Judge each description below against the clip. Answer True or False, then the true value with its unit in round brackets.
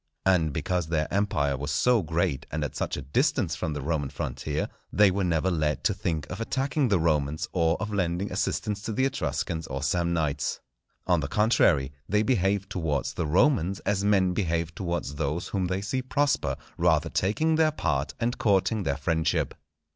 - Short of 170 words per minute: False (180 wpm)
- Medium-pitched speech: False (85 Hz)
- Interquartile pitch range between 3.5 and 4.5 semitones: False (5.0 semitones)